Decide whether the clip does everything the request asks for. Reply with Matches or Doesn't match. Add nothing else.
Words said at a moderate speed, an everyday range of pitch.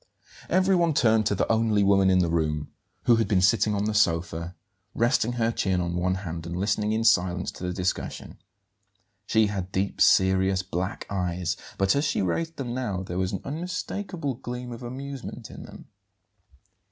Matches